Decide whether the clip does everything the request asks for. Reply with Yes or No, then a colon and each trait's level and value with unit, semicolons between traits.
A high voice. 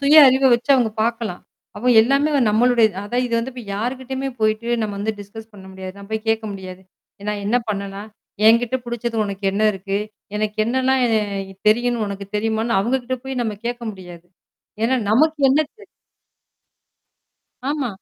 Yes: high, 225 Hz